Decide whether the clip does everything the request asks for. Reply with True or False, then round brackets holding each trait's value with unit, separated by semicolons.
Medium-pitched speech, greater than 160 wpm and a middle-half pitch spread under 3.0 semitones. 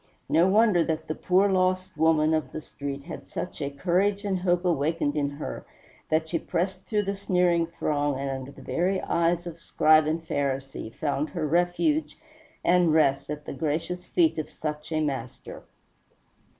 False (160 Hz; 175 wpm; 3.5 semitones)